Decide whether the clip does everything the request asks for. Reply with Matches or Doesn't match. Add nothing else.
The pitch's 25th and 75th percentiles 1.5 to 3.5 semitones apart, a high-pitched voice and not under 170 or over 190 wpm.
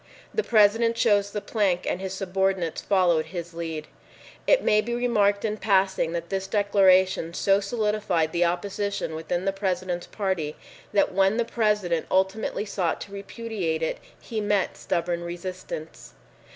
Doesn't match